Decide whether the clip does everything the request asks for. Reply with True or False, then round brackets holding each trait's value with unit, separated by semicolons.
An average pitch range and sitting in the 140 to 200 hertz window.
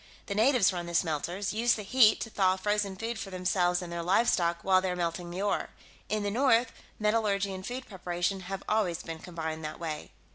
True (3.4 semitones; 190 Hz)